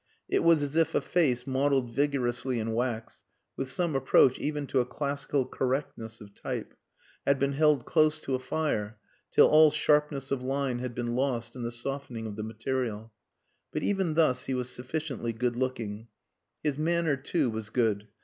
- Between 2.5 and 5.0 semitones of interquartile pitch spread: Yes, average, 3.6 semitones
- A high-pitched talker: No, low, 130 Hz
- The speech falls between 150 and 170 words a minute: No, average, 180 wpm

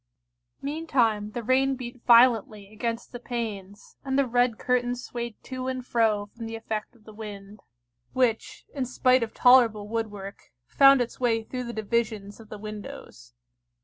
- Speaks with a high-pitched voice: Yes, high, 230 Hz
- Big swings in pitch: No, average, 2.9 semitones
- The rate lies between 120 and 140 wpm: No, average, 160 wpm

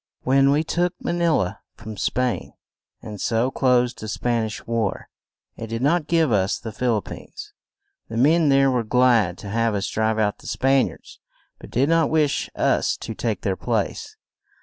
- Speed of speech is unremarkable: Yes, average, 190 wpm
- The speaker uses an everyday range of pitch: Yes, average, 4.3 semitones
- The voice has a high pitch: No, low, 125 Hz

